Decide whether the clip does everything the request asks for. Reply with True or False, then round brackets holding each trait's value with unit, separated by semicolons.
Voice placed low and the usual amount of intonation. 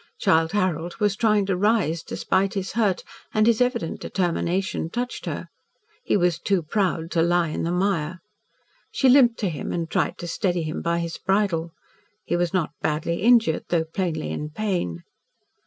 False (180 Hz; 3.7 semitones)